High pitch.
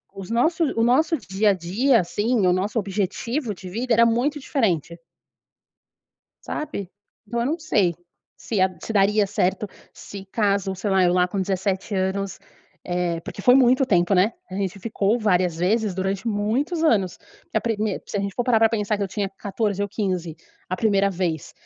Yes: high, 200 Hz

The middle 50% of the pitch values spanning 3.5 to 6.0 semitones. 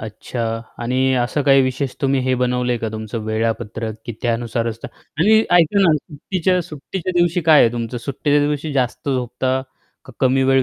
Yes: average, 3.9 semitones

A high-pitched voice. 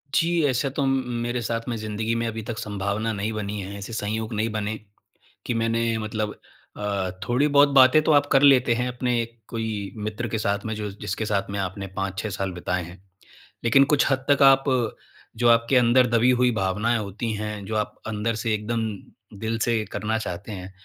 No: low, 110 Hz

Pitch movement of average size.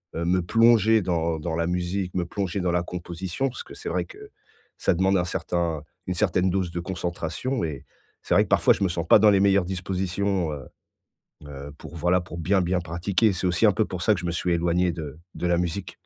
No: narrow, 2.2 semitones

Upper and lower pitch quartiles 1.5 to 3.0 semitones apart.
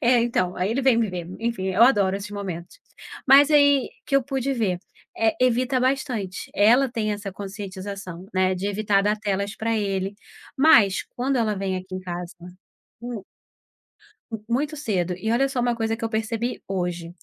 No: average, 4.4 semitones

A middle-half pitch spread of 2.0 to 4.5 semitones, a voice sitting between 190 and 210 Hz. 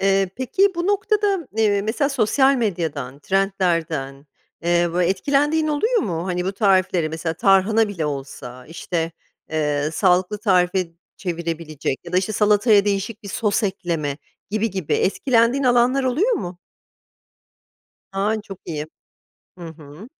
No: average, 5.2 semitones; high, 195 Hz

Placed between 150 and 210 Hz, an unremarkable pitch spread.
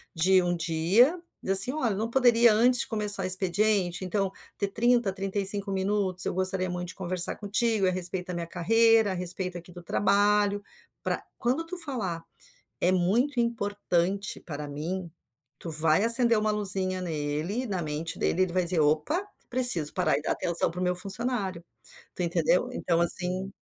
Yes: high, 190 Hz; average, 3.6 semitones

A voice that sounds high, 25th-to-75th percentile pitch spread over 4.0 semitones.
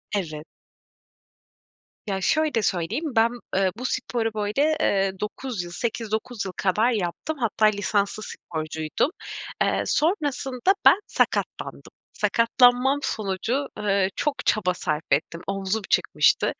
Yes: high, 215 Hz; average, 4.7 semitones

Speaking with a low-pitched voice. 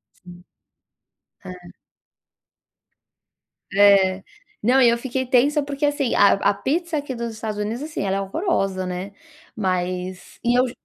No: high, 220 Hz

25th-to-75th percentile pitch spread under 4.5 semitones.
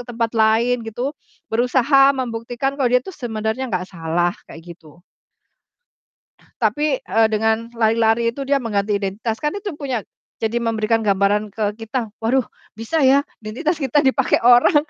Yes: average, 3.4 semitones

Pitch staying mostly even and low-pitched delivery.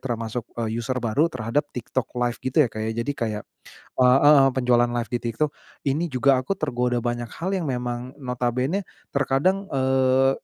Yes: narrow, 2.1 semitones; low, 125 Hz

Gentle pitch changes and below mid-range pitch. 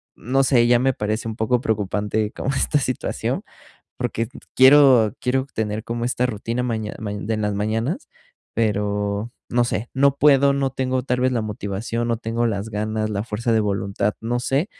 No: average, 3.2 semitones; low, 115 Hz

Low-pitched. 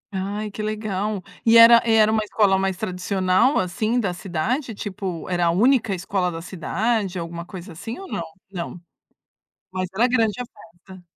No: high, 200 Hz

